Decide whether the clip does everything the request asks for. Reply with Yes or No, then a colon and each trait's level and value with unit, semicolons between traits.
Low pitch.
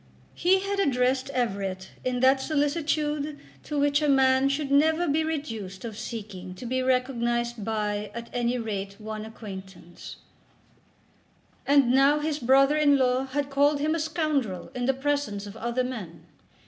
No: very high, 260 Hz